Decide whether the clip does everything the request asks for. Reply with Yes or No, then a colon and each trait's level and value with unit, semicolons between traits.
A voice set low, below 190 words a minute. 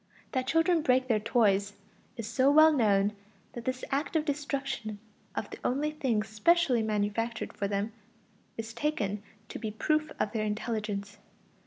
No: high, 230 Hz; average, 160 wpm